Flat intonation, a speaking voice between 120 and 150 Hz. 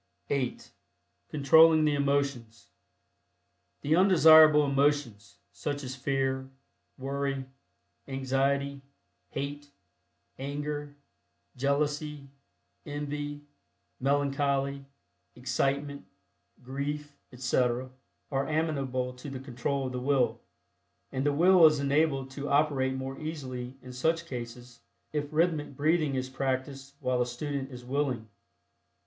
Yes: narrow, 1.9 semitones; medium, 140 Hz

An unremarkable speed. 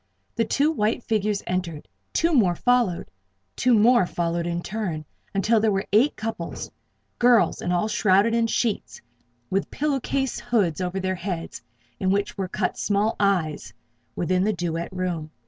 Yes: average, 160 wpm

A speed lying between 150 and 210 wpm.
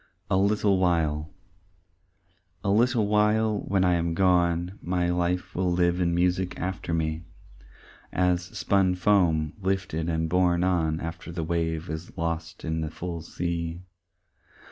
No: average, 140 wpm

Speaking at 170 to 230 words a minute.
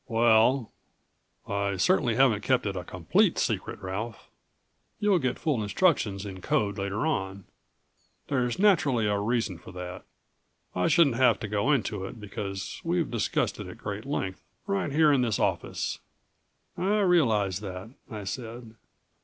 No: average, 150 wpm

